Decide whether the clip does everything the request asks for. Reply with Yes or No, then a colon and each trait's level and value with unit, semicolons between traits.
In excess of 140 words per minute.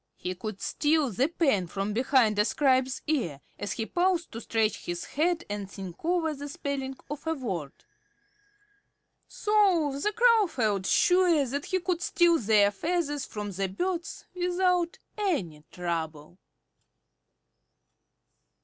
No: slow, 135 wpm